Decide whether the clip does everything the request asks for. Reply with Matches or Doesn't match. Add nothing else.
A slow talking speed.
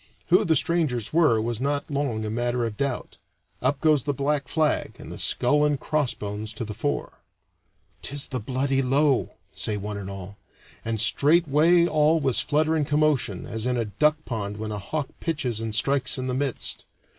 Doesn't match